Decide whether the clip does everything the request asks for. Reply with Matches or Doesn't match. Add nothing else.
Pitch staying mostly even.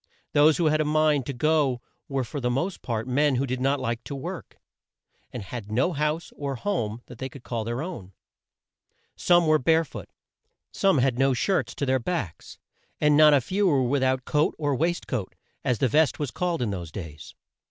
Doesn't match